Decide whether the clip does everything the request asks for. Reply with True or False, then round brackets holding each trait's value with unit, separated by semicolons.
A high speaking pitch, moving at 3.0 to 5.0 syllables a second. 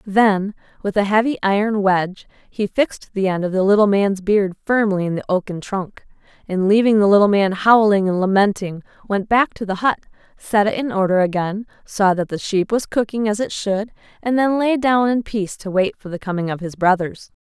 False (205 Hz; 5.3 syllables/s)